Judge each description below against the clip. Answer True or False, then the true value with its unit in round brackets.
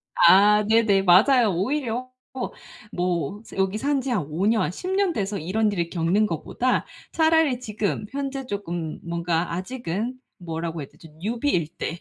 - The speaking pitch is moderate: False (205 Hz)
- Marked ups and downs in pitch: True (6.4 semitones)